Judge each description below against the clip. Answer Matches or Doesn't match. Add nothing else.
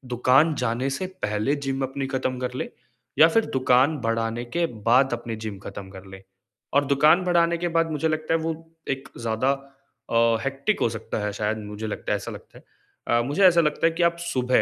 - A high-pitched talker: Doesn't match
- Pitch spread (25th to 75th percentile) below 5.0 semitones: Doesn't match